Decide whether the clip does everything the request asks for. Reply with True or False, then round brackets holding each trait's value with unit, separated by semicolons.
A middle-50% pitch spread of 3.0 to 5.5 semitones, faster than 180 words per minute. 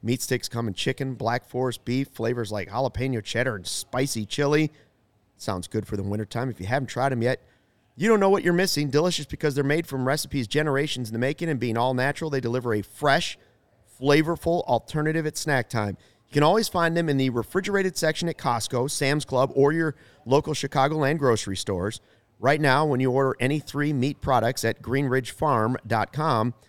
True (4.1 semitones; 195 wpm)